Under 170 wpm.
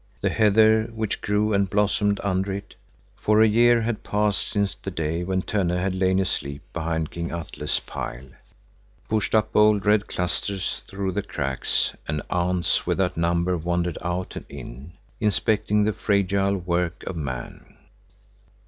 Yes: average, 150 wpm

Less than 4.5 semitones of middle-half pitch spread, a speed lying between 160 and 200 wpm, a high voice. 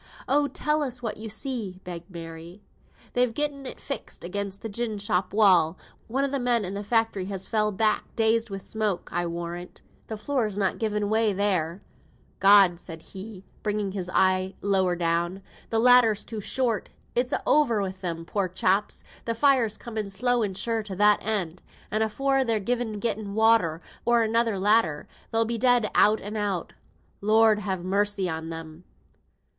Yes: average, 3.4 semitones; average, 175 wpm; high, 210 Hz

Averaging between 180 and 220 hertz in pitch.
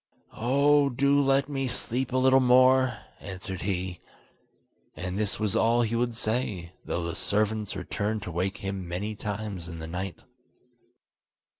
No: low, 110 Hz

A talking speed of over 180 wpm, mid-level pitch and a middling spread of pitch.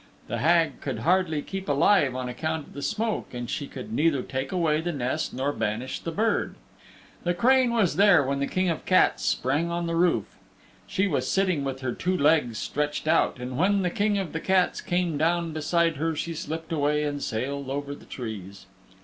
Yes: fast, 205 wpm; medium, 155 Hz; average, 4.3 semitones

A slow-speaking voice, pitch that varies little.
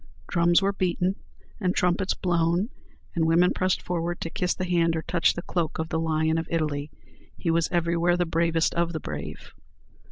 No: average, 185 wpm; narrow, 1.5 semitones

